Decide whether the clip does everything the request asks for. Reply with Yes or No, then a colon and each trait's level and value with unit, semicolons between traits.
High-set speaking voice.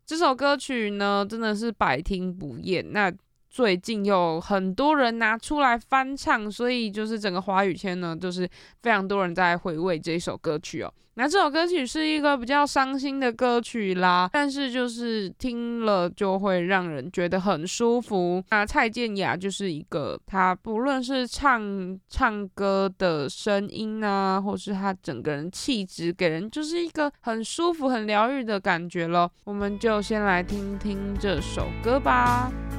Yes: high, 205 Hz